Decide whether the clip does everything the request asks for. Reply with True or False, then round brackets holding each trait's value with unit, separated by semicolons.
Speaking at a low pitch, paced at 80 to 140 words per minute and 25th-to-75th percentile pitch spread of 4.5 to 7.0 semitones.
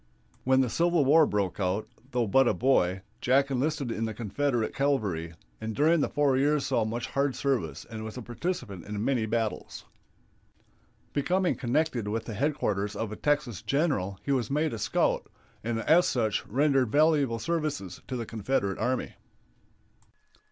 False (125 Hz; 165 wpm; 5.0 semitones)